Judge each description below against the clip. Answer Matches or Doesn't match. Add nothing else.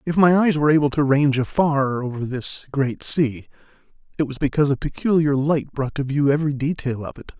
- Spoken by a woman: Doesn't match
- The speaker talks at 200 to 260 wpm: Matches